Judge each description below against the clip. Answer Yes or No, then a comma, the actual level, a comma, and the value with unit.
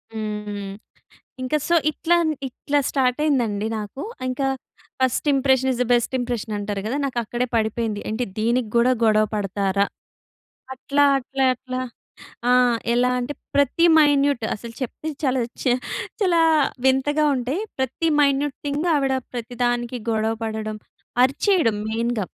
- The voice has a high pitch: Yes, very high, 250 Hz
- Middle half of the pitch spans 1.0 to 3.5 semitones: No, average, 3.9 semitones